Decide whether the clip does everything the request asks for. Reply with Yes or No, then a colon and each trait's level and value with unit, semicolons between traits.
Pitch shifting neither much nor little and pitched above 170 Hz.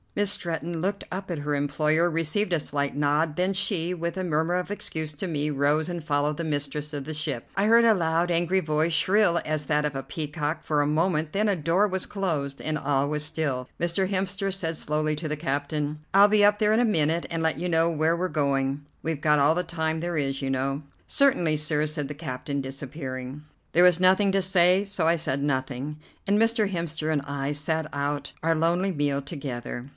No: average, 3.5 semitones; medium, 160 Hz